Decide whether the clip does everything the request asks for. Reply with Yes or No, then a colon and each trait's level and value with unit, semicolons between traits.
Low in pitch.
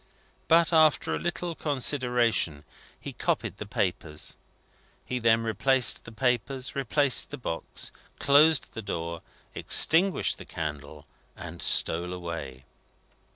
Yes: low, 120 Hz